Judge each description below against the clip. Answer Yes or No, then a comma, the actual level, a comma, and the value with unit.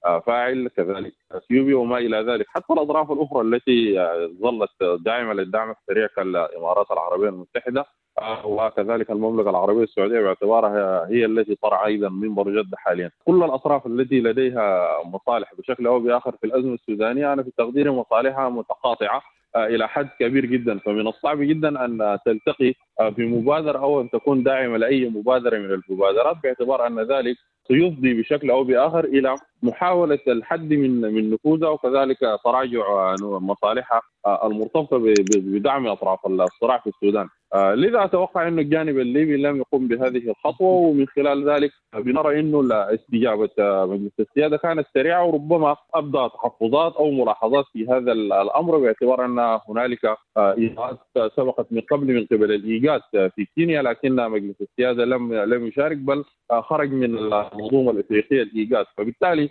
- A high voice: No, low, 125 Hz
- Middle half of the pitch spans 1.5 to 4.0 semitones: No, average, 4.7 semitones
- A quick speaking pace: Yes, fast, 140 wpm